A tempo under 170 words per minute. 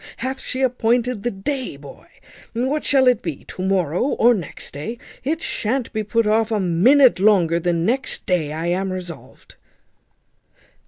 Yes: average, 160 wpm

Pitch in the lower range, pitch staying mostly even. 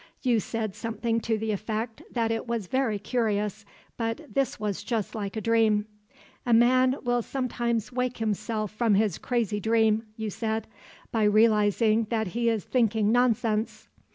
No: high, 225 Hz; narrow, 1.8 semitones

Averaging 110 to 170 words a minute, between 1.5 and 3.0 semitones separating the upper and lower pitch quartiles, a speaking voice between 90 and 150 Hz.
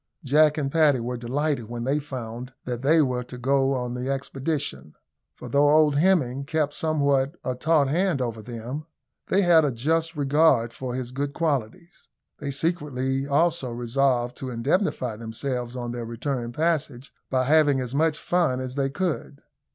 No: average, 165 wpm; average, 3.5 semitones; low, 135 Hz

